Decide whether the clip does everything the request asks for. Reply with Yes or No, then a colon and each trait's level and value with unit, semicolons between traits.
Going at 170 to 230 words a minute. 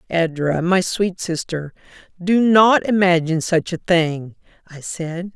No: slow, 135 wpm